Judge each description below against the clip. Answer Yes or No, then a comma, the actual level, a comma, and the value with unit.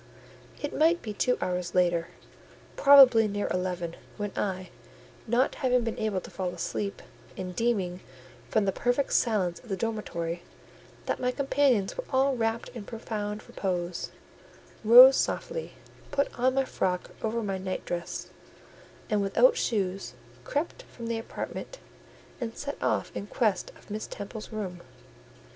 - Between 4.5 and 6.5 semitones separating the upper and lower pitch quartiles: Yes, average, 5.1 semitones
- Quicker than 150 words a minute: No, average, 140 wpm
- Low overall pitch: No, high, 215 Hz